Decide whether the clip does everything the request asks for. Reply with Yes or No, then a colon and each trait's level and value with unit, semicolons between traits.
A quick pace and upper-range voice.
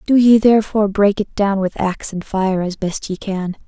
Yes: fast, 230 wpm; high, 200 Hz